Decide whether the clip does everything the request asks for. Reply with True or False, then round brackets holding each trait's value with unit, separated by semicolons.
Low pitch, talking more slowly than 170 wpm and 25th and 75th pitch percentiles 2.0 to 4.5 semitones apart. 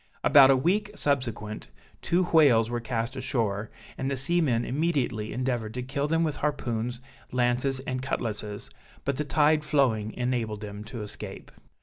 True (125 Hz; 150 wpm; 4.1 semitones)